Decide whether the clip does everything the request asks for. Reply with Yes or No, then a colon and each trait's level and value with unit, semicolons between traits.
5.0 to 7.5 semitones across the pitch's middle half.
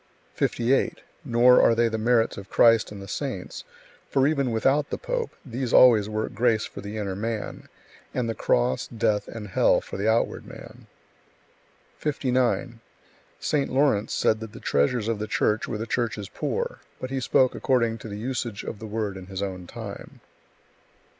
No: average, 3.2 semitones